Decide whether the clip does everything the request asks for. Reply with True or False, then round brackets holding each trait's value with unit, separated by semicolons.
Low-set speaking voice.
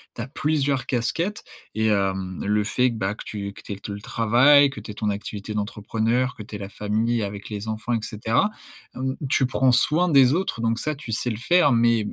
True (115 Hz)